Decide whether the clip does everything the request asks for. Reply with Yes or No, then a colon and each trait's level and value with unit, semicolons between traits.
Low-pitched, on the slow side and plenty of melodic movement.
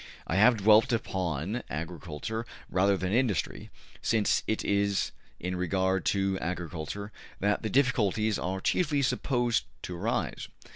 No: low, 100 Hz; slow, 130 wpm; average, 3.4 semitones